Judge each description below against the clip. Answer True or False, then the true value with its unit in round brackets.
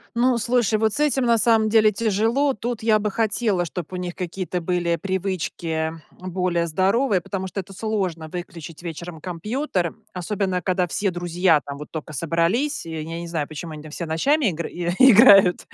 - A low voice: False (185 Hz)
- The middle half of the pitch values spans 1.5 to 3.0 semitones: False (4.5 semitones)